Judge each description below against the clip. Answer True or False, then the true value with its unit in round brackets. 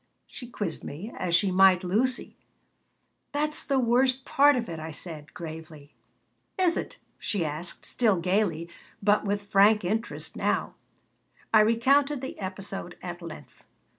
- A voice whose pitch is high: True (200 Hz)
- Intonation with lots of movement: True (5.9 semitones)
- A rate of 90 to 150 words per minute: True (140 wpm)